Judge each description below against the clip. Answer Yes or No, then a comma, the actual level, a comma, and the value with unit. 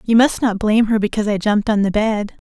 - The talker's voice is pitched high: Yes, high, 215 Hz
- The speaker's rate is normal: No, fast, 265 wpm